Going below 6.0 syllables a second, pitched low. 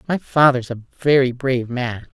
Yes: 4.9 syllables/s; low, 130 Hz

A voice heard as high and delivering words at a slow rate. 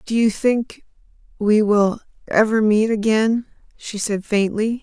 Yes: high, 215 Hz; slow, 110 wpm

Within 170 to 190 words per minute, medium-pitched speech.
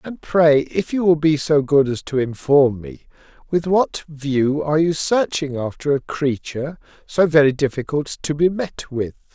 Yes: average, 180 wpm; medium, 150 Hz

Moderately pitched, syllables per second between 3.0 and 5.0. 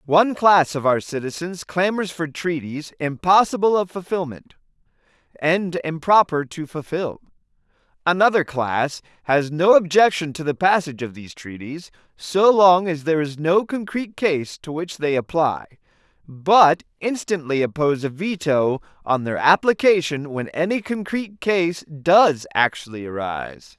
Yes: medium, 165 Hz; 4.6 syllables/s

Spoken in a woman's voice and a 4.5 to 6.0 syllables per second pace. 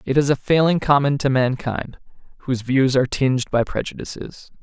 No: male; 5.6 syllables/s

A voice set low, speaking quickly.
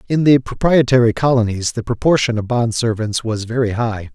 No: low, 120 Hz; average, 175 wpm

